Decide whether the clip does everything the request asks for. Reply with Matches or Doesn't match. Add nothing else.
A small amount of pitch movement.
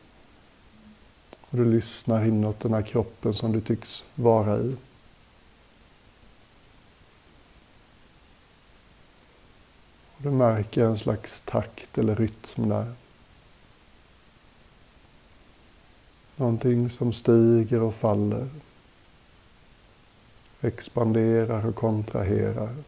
Matches